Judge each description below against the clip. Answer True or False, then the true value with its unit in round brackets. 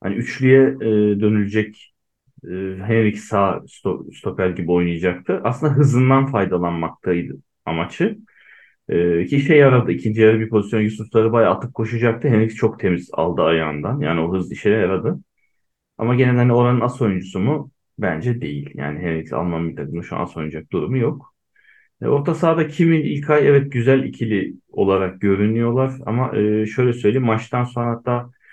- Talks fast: True (145 wpm)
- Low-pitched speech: True (110 Hz)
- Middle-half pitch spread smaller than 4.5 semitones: False (5.3 semitones)